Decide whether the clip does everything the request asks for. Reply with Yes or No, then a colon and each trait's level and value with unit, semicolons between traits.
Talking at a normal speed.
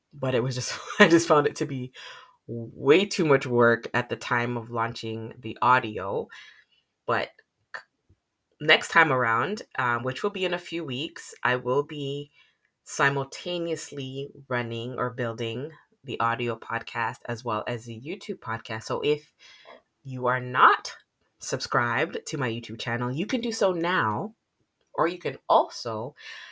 Yes: average, 155 wpm